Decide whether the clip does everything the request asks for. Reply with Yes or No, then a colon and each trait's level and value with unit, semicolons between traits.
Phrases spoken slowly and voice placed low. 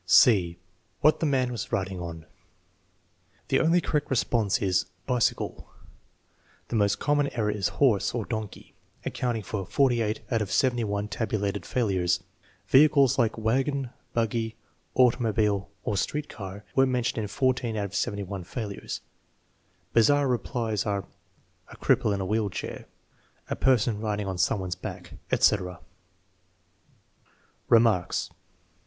Yes: slow, 130 wpm; low, 110 Hz